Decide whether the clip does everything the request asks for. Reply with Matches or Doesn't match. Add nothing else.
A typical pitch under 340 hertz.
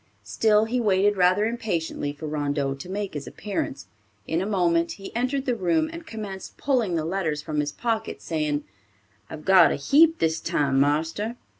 Matches